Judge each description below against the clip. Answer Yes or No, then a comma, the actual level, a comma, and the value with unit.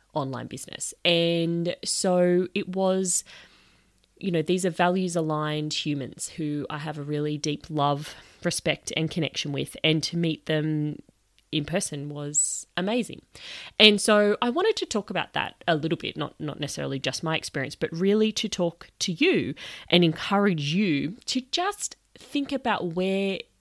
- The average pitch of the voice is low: No, medium, 170 Hz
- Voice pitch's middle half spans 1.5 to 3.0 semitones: No, average, 4.2 semitones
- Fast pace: No, average, 160 wpm